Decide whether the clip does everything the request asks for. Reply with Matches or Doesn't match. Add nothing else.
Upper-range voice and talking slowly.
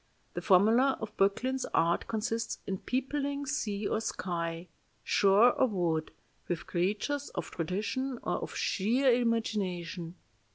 Matches